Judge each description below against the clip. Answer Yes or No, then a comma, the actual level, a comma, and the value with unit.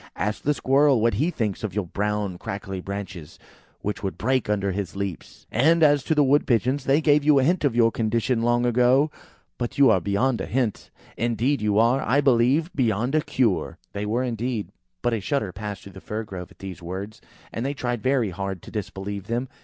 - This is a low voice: Yes, low, 115 Hz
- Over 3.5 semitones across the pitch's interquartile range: Yes, average, 4.8 semitones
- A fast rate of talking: Yes, fast, 210 wpm